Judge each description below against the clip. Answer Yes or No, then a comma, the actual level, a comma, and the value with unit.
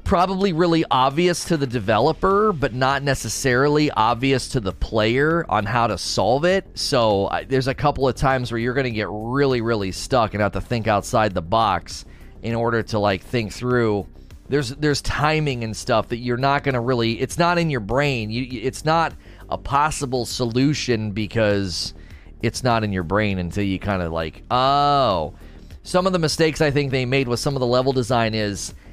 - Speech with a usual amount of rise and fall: Yes, average, 5.0 semitones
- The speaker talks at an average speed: Yes, average, 195 wpm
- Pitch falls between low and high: No, low, 125 Hz